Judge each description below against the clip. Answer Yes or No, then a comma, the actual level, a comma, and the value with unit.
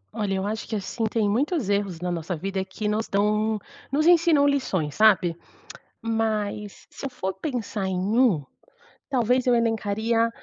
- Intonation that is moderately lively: Yes, average, 3.5 semitones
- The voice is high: Yes, high, 215 Hz